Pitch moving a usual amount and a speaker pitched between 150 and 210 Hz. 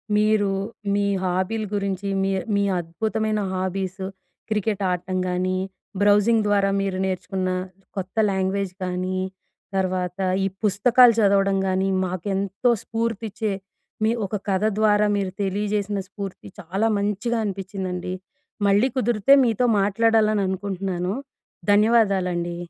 No: narrow, 2.2 semitones; high, 195 Hz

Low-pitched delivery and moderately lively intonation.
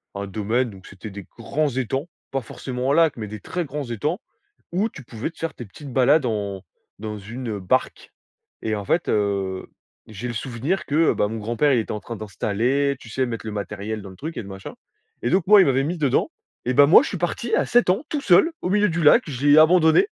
No: low, 125 Hz; wide, 6.7 semitones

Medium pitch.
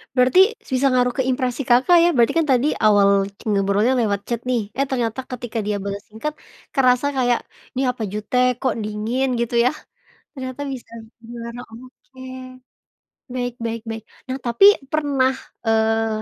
No: high, 245 Hz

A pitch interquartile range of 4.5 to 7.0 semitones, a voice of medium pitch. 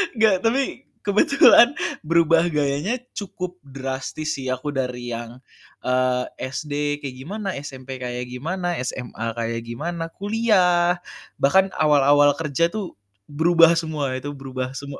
Yes: average, 5.2 semitones; medium, 145 Hz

